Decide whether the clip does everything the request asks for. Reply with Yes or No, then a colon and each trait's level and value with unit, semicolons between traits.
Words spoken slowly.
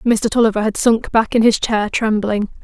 No: fast, 205 wpm